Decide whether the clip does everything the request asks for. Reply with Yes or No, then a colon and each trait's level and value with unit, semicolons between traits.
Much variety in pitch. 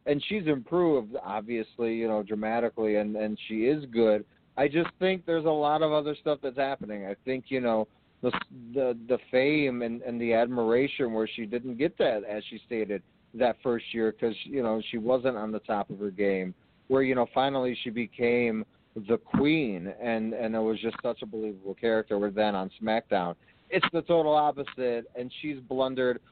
No: average, 3.3 semitones